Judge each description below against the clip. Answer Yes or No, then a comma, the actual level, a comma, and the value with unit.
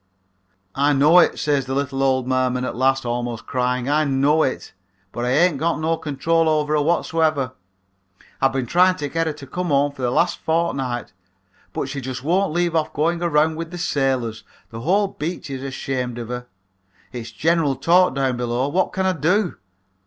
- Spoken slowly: No, average, 190 wpm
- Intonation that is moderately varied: Yes, average, 4.1 semitones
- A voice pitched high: No, medium, 140 Hz